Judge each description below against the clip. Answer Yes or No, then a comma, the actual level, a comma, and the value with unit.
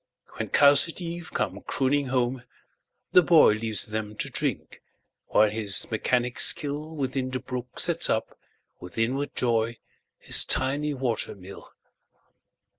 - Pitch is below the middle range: Yes, low, 130 Hz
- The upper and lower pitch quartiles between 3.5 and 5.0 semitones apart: Yes, average, 4.2 semitones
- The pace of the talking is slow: Yes, slow, 120 wpm